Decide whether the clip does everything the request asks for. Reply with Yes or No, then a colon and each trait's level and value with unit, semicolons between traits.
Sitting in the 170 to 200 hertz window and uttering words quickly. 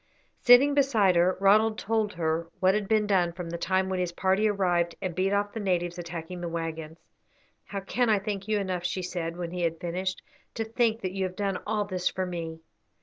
Yes: medium, 185 Hz; fast, 215 wpm